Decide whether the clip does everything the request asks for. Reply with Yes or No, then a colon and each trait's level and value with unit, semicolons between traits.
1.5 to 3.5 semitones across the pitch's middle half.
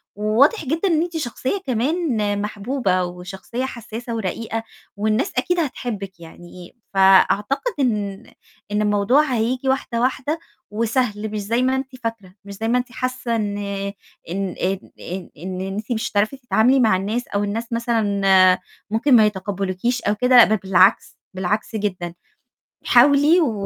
No: average, 4.2 semitones